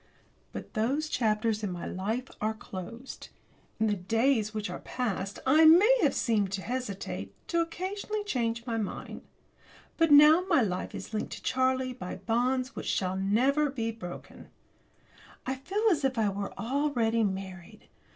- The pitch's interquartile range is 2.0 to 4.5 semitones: No, average, 5.1 semitones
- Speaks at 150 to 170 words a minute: Yes, average, 160 wpm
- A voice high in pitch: Yes, high, 230 Hz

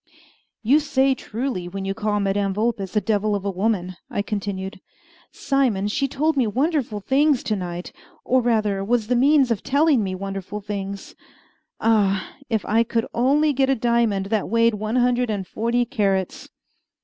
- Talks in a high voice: Yes, high, 220 Hz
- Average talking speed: Yes, average, 170 wpm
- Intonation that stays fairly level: No, average, 4.2 semitones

